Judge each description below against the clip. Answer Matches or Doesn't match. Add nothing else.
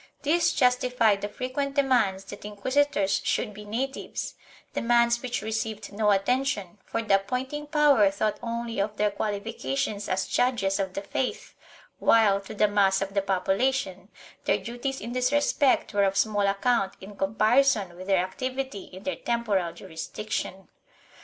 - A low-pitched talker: Doesn't match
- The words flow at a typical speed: Matches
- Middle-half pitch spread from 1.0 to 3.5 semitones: Doesn't match